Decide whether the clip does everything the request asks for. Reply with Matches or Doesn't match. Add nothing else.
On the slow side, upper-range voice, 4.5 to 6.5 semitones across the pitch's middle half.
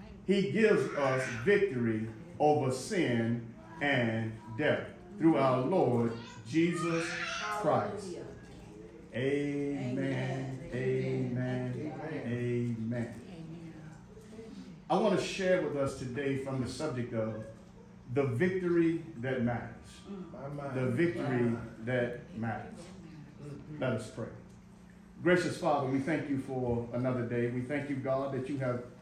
Doesn't match